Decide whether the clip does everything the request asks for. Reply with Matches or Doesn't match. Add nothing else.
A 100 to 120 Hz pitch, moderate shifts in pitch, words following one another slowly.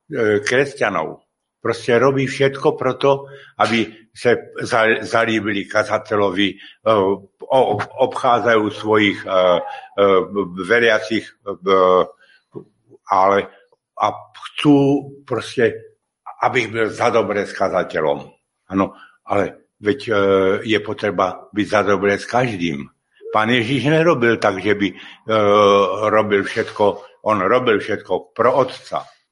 Matches